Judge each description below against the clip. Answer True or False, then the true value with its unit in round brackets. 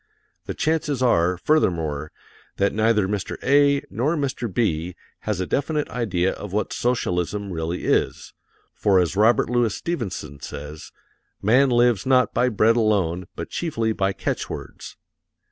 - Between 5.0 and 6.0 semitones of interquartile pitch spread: True (5.6 semitones)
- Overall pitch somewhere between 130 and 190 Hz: False (105 Hz)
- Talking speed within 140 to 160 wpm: True (145 wpm)